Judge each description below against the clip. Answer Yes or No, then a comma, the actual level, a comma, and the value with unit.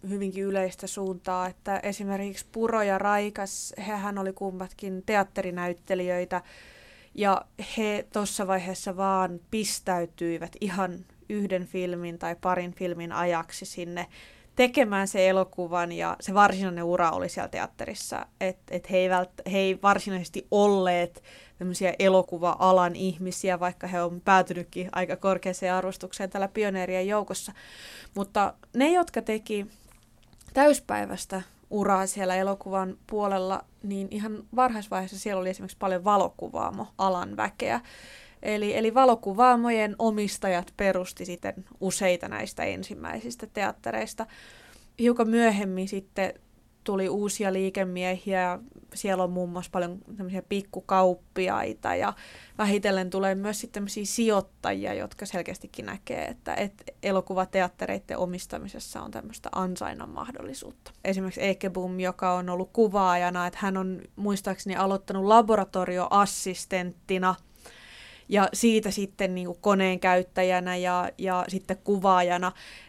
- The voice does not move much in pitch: Yes, narrow, 1.9 semitones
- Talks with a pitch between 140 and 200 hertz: Yes, high, 190 Hz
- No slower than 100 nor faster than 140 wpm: Yes, average, 115 wpm